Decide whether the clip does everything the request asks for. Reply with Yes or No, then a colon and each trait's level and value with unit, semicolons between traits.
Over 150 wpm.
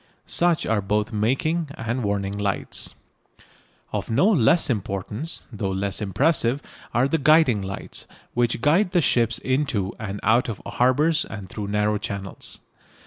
No: average, 140 wpm